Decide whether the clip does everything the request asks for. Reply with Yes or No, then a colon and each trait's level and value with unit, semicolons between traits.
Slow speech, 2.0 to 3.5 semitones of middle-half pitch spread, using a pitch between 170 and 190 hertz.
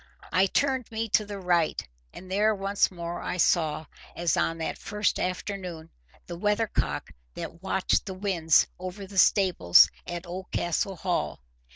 No: average, 150 wpm; average, 2.8 semitones; medium, 185 Hz